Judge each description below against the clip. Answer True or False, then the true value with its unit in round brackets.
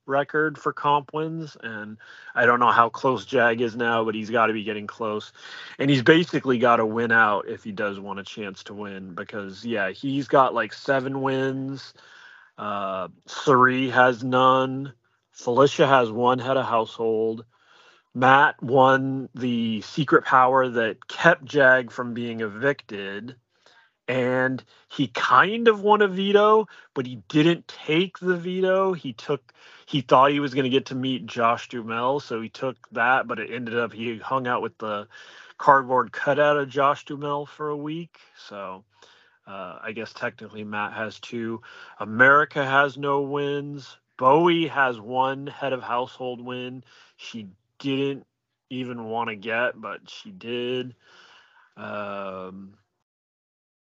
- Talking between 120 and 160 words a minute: True (155 wpm)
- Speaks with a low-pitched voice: True (130 Hz)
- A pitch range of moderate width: True (3.7 semitones)